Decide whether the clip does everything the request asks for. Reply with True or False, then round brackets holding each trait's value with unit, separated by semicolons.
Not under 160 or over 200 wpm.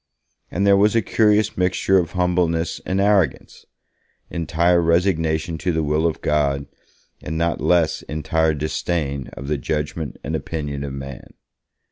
False (145 wpm)